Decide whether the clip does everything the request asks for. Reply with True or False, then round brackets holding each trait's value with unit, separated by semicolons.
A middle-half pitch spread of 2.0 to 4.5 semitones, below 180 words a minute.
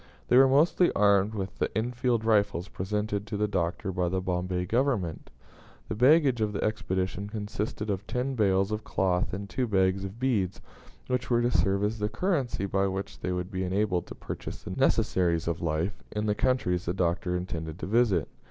False (3.3 semitones; 190 wpm)